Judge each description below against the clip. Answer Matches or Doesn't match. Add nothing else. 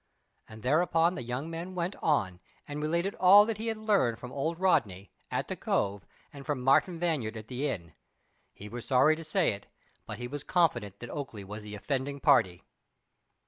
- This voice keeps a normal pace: Matches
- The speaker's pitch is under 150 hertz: Matches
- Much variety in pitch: Matches